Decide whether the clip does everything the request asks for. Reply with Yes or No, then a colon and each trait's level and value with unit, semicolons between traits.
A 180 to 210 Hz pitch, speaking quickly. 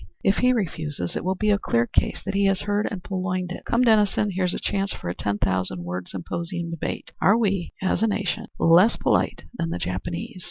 Yes: medium, 185 Hz; fast, 215 wpm